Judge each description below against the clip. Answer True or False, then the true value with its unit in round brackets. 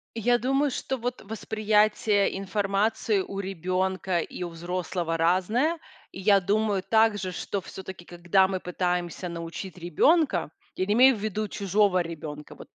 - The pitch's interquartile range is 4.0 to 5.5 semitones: False (3.3 semitones)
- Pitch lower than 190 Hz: False (195 Hz)